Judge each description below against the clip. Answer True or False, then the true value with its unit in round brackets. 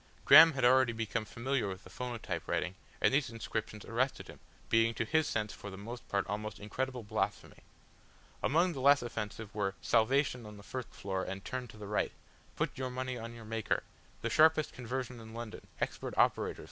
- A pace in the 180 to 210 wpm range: True (190 wpm)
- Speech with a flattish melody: False (3.5 semitones)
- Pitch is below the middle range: True (115 Hz)